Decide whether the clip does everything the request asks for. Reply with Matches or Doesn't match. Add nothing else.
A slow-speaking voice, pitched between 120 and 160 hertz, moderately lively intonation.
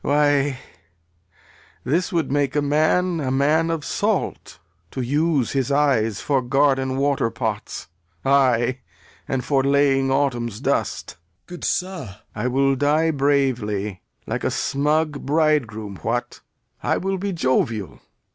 Matches